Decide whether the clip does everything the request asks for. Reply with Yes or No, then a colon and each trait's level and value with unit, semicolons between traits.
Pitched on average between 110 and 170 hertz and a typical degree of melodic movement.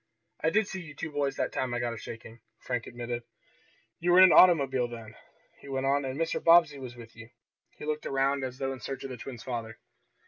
Yes: low, 135 Hz; average, 3.7 semitones